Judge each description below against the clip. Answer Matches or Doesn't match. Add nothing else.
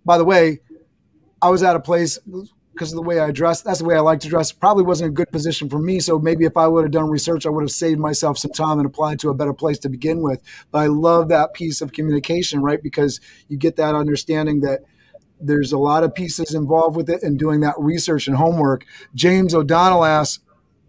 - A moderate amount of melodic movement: Doesn't match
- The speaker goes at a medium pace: Doesn't match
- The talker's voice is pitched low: Doesn't match